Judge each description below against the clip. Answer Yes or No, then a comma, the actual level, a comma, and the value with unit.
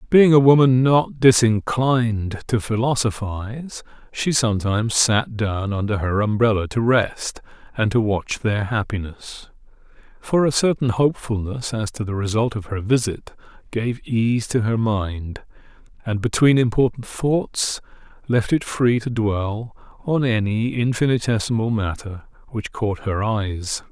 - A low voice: Yes, low, 115 Hz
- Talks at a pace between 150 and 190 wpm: No, slow, 135 wpm